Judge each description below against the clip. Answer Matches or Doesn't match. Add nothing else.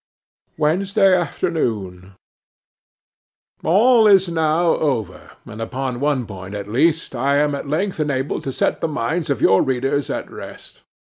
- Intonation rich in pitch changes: Matches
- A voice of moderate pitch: Matches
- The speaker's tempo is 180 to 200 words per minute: Doesn't match